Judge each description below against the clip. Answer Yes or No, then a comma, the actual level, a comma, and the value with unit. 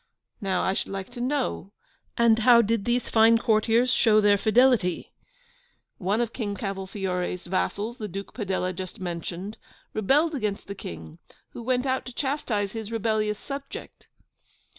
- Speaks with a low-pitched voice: No, high, 215 Hz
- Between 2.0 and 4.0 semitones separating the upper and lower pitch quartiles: Yes, average, 3.6 semitones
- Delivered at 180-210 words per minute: No, average, 150 wpm